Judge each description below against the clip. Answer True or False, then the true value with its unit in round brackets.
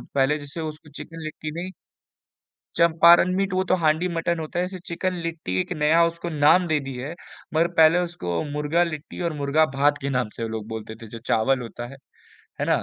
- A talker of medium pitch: True (155 Hz)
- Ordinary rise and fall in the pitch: True (3.5 semitones)